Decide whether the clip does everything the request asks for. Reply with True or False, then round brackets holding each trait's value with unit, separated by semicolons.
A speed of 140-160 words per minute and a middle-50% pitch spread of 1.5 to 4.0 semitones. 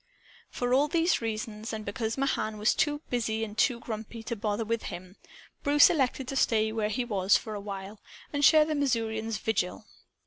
False (185 wpm; 3.6 semitones)